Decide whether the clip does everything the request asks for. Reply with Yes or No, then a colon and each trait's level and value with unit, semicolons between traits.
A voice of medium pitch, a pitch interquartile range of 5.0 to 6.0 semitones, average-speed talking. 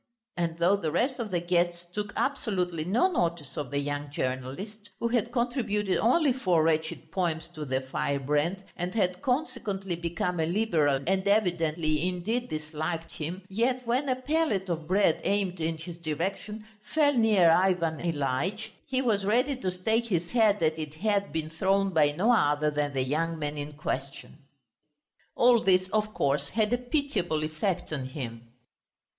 Yes: medium, 180 Hz; wide, 5.6 semitones; average, 165 wpm